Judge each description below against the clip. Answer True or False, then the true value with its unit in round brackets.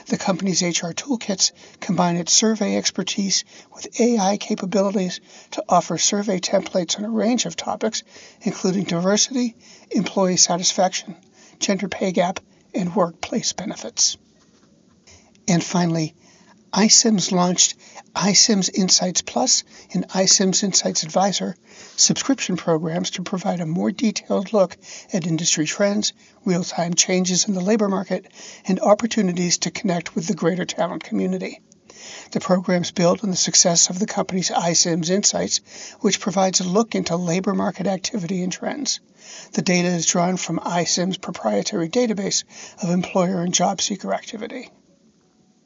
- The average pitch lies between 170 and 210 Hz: True (190 Hz)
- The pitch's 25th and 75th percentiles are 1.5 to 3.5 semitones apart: True (2.8 semitones)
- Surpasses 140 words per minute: False (135 wpm)